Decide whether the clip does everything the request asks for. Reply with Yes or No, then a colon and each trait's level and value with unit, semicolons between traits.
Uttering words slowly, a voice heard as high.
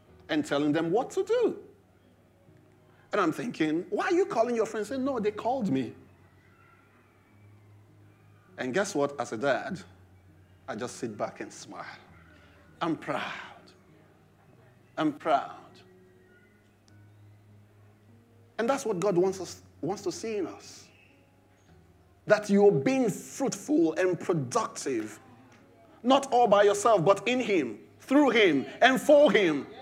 No: slow, 130 wpm; low, 135 Hz